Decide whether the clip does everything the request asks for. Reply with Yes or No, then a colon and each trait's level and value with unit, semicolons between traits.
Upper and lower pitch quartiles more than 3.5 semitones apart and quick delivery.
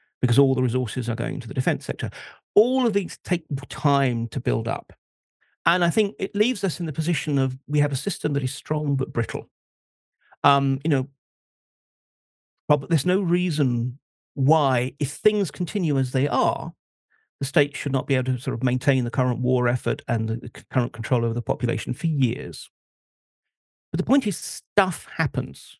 Yes: average, 4.5 semitones; fast, 185 wpm